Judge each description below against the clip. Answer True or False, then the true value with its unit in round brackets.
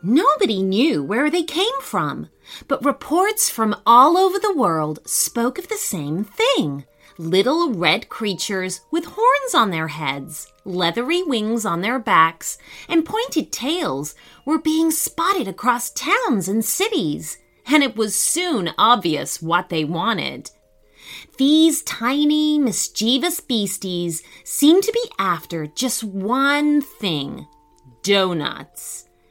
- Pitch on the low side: False (230 Hz)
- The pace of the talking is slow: True (125 wpm)